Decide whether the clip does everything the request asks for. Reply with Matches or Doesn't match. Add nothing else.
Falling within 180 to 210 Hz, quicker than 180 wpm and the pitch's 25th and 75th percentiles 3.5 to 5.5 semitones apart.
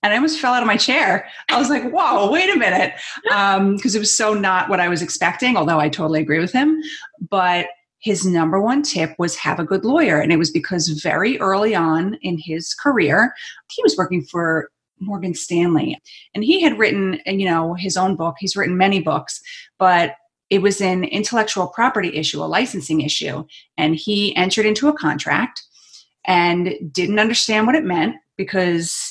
Matches